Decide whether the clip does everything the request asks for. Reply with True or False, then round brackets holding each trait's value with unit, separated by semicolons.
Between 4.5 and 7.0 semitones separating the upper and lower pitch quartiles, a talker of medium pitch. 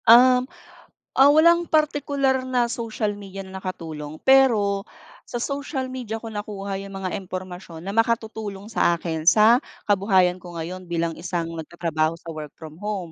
False (5.5 semitones; 195 Hz)